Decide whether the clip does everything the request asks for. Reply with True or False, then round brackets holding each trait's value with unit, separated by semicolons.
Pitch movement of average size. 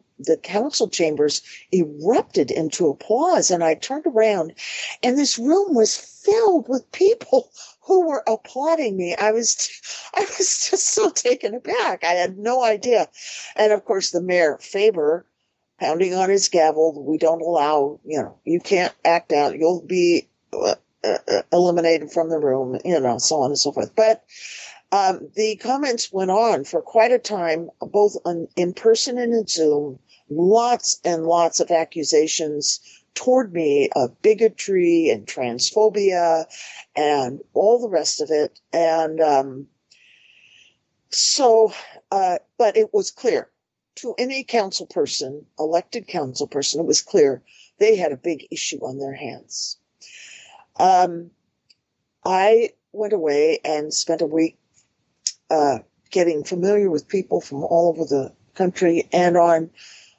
False (7.3 semitones)